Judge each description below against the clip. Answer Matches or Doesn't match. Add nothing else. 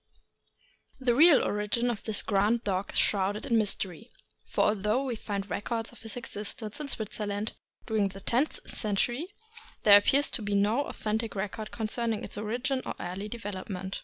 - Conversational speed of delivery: Matches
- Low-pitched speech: Doesn't match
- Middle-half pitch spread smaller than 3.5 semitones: Matches